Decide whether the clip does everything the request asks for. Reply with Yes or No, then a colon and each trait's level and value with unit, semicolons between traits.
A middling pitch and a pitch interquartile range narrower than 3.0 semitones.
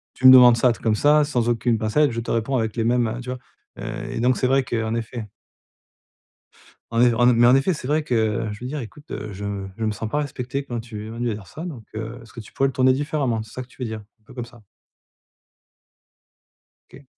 No: low, 120 Hz; narrow, 2.6 semitones